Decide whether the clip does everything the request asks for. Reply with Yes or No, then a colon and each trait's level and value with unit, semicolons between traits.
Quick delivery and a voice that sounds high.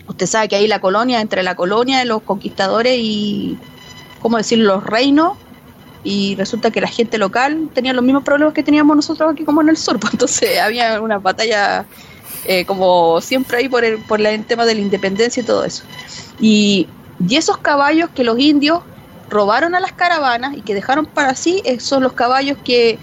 Yes: fast, 195 wpm; high, 235 Hz